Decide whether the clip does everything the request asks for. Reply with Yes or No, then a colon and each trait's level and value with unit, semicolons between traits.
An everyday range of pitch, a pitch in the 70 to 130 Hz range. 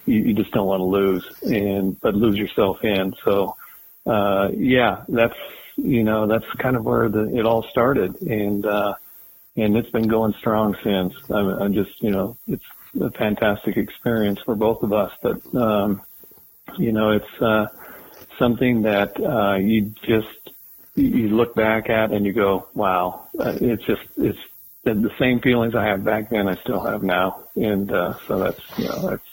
No: narrow, 2.2 semitones; low, 105 Hz